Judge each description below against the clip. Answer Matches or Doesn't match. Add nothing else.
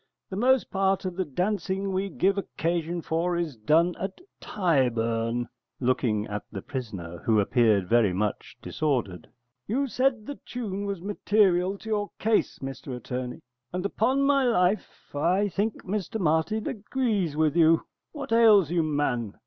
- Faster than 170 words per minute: Doesn't match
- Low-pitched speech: Doesn't match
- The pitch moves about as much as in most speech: Doesn't match